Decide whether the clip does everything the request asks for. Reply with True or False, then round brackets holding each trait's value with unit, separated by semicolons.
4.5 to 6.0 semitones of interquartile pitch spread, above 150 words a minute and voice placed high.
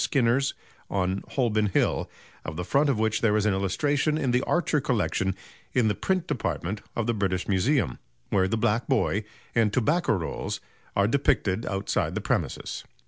False (5.4 semitones; 170 wpm; 110 Hz)